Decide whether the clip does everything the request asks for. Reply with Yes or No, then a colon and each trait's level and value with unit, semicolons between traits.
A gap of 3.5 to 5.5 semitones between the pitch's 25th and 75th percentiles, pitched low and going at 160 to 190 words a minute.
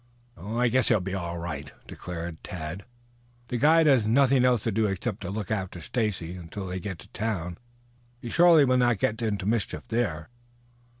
Yes: average, 5.2 semitones; low, 105 Hz; average, 185 wpm